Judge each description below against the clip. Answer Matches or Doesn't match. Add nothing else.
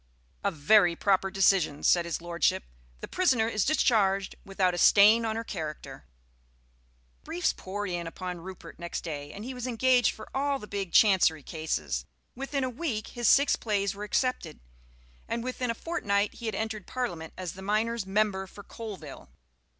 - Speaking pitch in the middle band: Doesn't match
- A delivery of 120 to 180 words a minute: Matches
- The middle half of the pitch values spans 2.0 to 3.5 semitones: Doesn't match